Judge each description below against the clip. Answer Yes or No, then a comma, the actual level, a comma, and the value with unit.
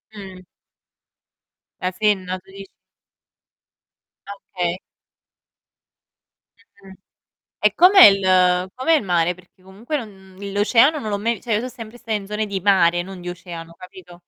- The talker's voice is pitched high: Yes, high, 195 Hz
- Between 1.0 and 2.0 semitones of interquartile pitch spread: No, average, 2.8 semitones